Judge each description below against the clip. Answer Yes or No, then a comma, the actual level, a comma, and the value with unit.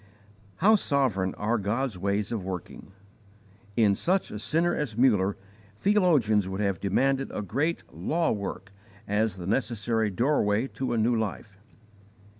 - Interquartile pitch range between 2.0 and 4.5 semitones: No, average, 5.3 semitones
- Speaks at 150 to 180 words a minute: No, average, 140 wpm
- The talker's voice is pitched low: Yes, low, 110 Hz